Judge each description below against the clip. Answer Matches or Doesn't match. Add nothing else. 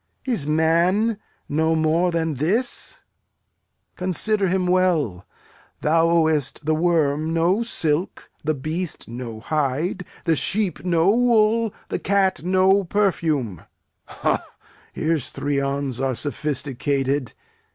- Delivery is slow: Matches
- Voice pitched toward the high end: Doesn't match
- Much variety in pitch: Doesn't match